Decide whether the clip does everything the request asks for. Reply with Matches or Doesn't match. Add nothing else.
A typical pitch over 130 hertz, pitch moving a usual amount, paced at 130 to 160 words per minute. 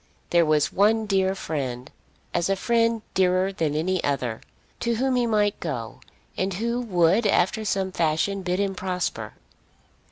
Matches